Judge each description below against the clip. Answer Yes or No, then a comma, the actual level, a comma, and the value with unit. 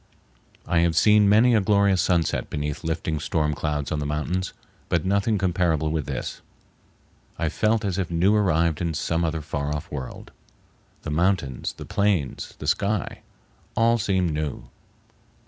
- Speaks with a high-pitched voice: No, very low, 85 Hz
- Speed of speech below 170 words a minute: Yes, average, 155 wpm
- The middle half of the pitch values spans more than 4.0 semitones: Yes, average, 4.5 semitones